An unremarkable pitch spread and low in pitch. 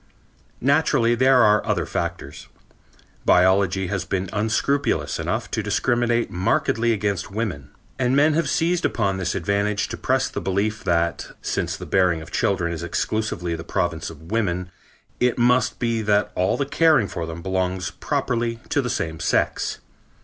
Yes: average, 5.0 semitones; low, 100 Hz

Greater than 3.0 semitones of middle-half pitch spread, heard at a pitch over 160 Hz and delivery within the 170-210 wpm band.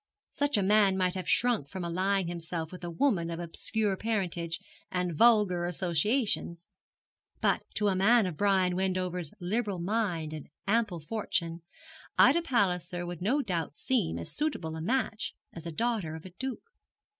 No: average, 4.2 semitones; medium, 185 Hz; average, 160 wpm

